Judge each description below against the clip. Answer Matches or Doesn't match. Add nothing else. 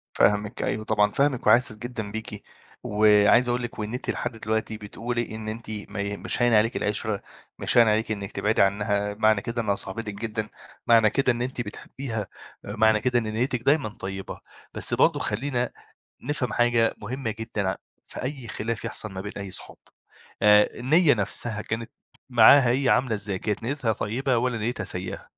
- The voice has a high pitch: Doesn't match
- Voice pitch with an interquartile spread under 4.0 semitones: Matches